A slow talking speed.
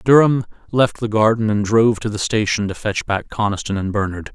No: fast, 205 wpm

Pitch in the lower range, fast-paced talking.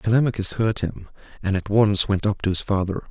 Yes: low, 100 Hz; fast, 210 wpm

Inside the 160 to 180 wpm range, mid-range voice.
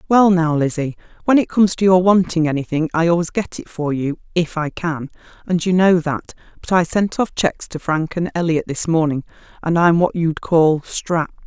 No: fast, 205 wpm; medium, 170 Hz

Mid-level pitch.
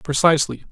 Yes: medium, 155 Hz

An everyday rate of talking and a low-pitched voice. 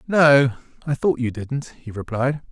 Yes: average, 165 wpm; low, 130 Hz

